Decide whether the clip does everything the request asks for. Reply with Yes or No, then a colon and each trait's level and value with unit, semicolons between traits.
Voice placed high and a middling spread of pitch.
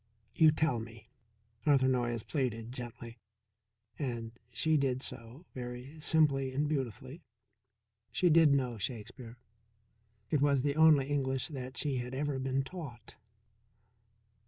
No: low, 130 Hz; average, 3.1 semitones